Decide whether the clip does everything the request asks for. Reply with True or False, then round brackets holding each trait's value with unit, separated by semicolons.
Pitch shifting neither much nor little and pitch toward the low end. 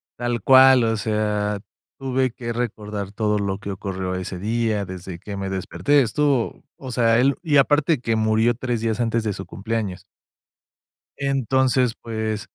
True (3.6 semitones; 115 Hz)